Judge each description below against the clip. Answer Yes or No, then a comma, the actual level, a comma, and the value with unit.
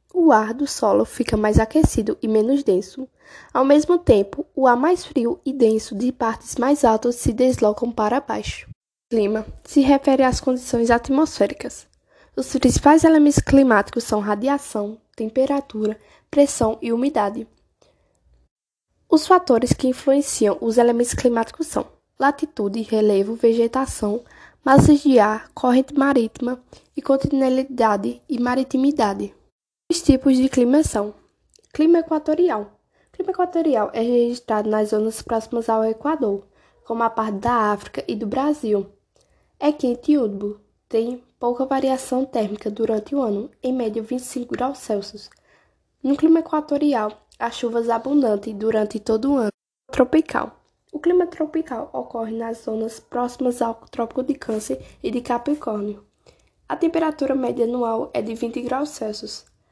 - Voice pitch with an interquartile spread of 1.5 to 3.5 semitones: No, average, 4.0 semitones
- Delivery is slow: No, average, 140 wpm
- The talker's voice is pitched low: No, high, 245 Hz